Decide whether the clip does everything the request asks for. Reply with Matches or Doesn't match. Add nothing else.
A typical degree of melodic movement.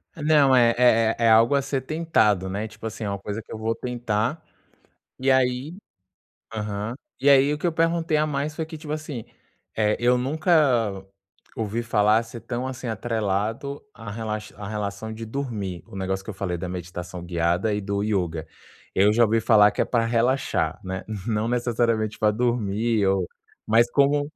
Matches